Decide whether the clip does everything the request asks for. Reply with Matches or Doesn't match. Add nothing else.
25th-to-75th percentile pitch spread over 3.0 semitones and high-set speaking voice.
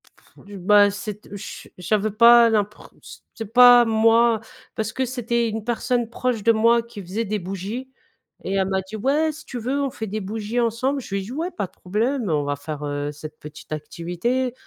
Matches